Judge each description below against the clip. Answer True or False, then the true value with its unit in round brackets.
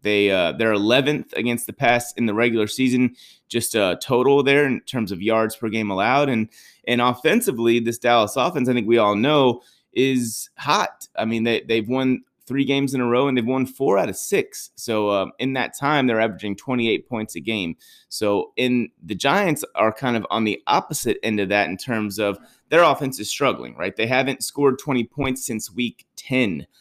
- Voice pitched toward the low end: True (120 Hz)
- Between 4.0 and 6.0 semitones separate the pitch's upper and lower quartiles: False (2.9 semitones)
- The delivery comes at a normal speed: False (210 wpm)